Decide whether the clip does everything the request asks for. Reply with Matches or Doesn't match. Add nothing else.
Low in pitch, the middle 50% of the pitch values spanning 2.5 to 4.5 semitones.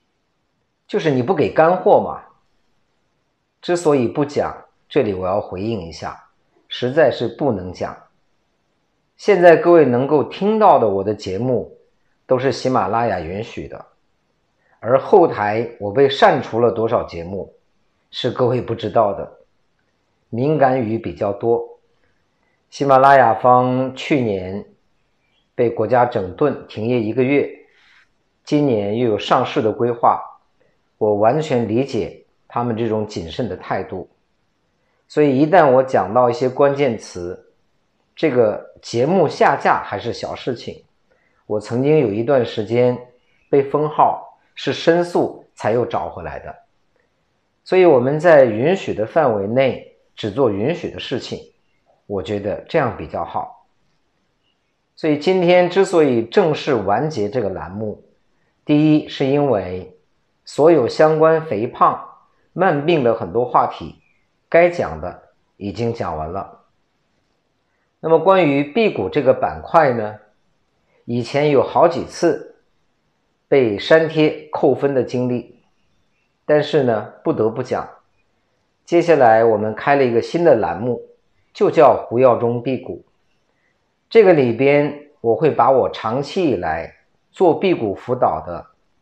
Doesn't match